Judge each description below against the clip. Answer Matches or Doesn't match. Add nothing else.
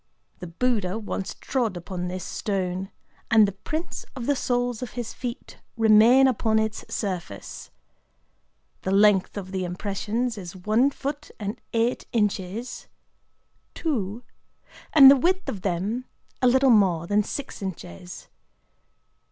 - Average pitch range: Matches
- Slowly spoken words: Matches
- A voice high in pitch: Matches